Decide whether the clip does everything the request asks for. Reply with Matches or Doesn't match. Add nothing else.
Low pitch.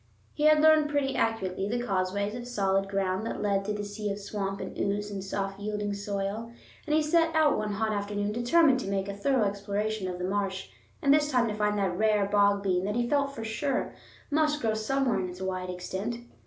Doesn't match